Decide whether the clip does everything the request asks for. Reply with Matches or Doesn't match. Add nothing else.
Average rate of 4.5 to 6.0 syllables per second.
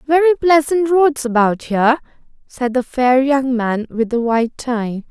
Doesn't match